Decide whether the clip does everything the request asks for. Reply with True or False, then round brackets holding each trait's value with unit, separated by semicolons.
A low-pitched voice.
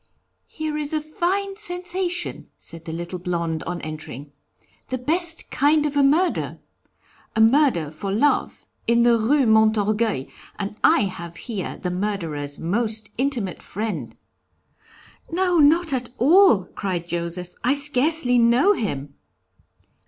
False (230 Hz)